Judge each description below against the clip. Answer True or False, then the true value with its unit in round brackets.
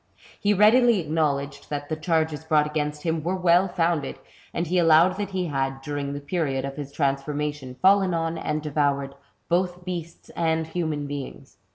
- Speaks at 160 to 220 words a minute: True (175 wpm)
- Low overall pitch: False (155 Hz)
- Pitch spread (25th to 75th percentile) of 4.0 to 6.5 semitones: False (3.5 semitones)